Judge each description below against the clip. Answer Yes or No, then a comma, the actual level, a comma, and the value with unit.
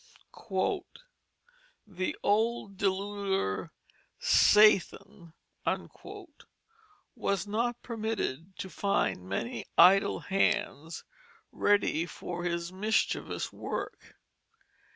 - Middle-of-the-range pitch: No, high, 195 Hz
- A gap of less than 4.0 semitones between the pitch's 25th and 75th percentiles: Yes, average, 3.4 semitones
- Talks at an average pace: No, slow, 70 wpm